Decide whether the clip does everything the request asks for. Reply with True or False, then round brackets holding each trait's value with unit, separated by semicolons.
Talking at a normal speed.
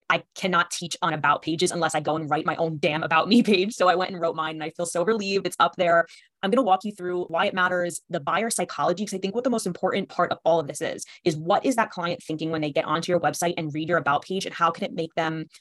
False (305 wpm)